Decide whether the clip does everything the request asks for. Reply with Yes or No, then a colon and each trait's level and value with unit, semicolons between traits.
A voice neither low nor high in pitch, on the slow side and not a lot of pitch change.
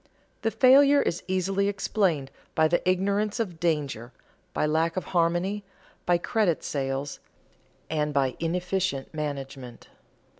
No: medium, 170 Hz; slow, 120 wpm; average, 4.8 semitones